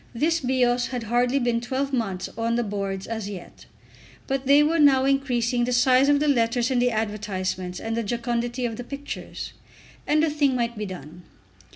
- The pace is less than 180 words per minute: No, average, 190 wpm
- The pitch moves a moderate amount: Yes, average, 3.2 semitones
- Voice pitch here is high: Yes, high, 240 Hz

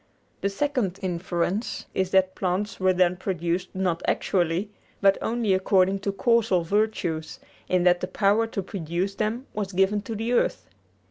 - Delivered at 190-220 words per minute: No, average, 155 wpm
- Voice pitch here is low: No, high, 190 Hz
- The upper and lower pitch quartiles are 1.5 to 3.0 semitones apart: Yes, narrow, 2.5 semitones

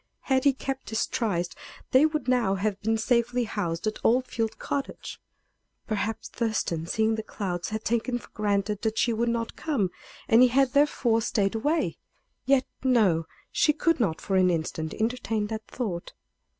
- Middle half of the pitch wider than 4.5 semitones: No, average, 3.8 semitones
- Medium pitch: No, high, 225 Hz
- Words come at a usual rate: Yes, average, 170 wpm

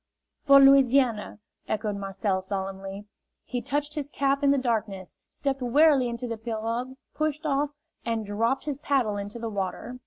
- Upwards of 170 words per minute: No, average, 155 wpm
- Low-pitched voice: No, high, 240 Hz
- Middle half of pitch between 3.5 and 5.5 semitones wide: Yes, average, 4.9 semitones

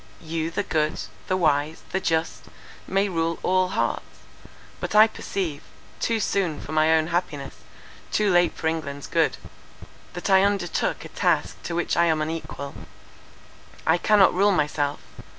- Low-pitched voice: No, medium, 165 Hz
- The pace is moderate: Yes, average, 150 wpm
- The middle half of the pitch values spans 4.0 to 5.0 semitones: No, average, 3.3 semitones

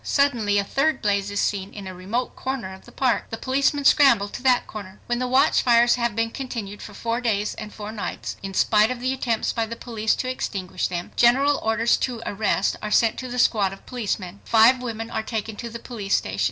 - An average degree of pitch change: Yes, average, 3.4 semitones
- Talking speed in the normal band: No, fast, 220 wpm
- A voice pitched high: Yes, high, 225 Hz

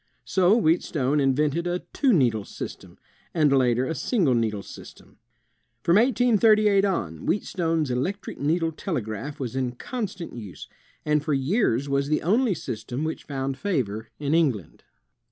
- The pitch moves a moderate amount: No, wide, 6.4 semitones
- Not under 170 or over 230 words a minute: No, average, 140 wpm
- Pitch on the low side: No, medium, 150 Hz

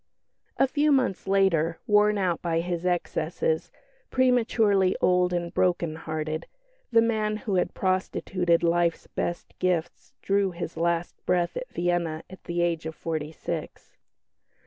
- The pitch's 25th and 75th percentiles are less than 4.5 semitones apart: Yes, average, 3.1 semitones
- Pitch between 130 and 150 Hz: No, medium, 180 Hz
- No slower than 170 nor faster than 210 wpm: No, average, 140 wpm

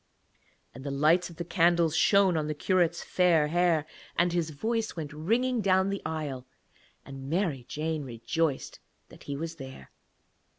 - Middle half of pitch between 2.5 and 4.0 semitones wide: Yes, average, 3.4 semitones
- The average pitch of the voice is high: No, medium, 165 Hz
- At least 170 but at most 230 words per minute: No, average, 160 wpm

